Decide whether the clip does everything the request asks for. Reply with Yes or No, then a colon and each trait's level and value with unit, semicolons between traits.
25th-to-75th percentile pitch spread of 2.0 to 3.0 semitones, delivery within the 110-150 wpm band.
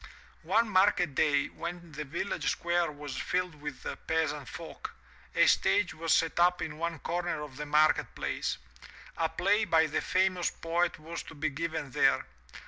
No: average, 2.7 semitones; average, 165 wpm